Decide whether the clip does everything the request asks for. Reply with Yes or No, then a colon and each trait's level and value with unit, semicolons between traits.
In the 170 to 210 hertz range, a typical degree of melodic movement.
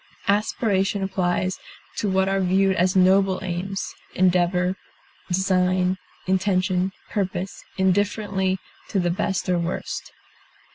No: high, 190 Hz; narrow, 1.1 semitones